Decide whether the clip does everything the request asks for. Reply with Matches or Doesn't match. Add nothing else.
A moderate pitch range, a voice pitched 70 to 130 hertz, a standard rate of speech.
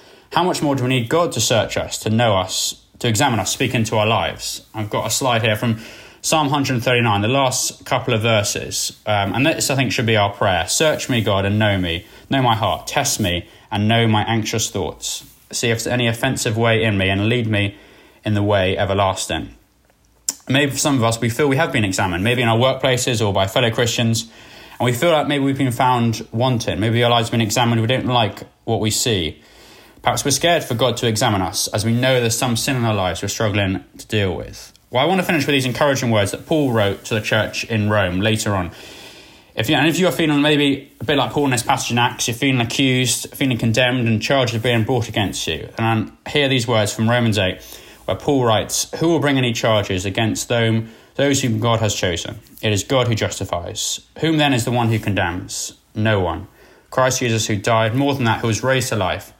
Doesn't match